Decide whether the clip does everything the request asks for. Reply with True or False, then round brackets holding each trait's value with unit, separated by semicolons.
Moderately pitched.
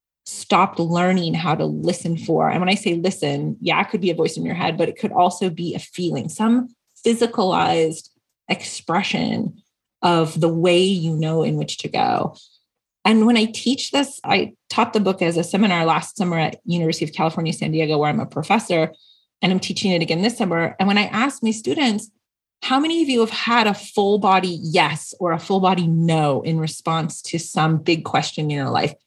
True (180 Hz)